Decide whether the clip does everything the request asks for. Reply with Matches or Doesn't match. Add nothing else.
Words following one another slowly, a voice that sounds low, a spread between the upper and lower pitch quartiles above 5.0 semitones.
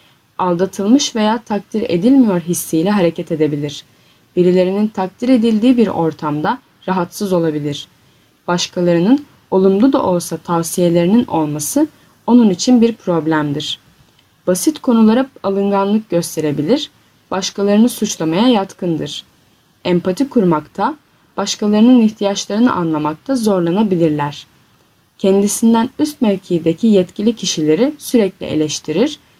Doesn't match